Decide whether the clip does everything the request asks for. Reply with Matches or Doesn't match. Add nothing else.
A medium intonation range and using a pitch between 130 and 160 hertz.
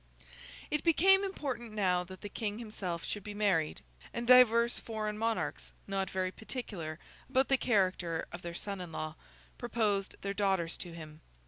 Doesn't match